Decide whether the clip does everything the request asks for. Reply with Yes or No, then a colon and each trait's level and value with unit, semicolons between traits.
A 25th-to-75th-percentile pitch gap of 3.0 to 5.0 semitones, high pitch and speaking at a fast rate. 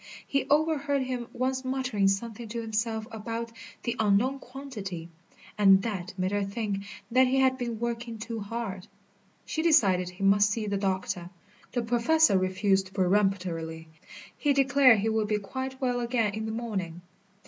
No: average, 4.4 semitones; high, 220 Hz; average, 160 wpm